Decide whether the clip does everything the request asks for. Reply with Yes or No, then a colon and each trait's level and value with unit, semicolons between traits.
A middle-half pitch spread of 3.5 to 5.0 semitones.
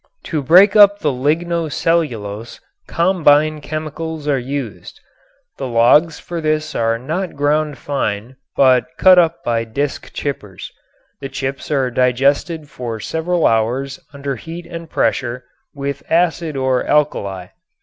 Yes: average, 4.3 semitones